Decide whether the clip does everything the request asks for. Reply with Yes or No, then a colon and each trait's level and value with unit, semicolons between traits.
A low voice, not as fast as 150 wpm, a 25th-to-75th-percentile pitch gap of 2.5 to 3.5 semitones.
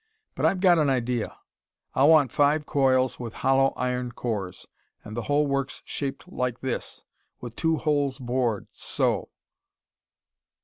Yes: low, 130 Hz; average, 140 wpm; average, 2.8 semitones